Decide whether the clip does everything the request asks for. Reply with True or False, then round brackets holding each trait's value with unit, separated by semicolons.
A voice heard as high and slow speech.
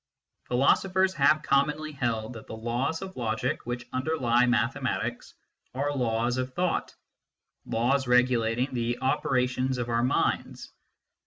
False (125 Hz; 125 wpm)